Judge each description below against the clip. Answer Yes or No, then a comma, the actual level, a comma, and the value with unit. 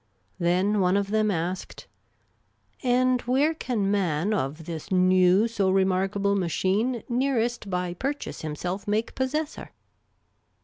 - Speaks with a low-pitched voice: No, high, 200 Hz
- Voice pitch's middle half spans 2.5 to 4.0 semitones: No, average, 4.7 semitones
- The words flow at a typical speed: No, slow, 130 wpm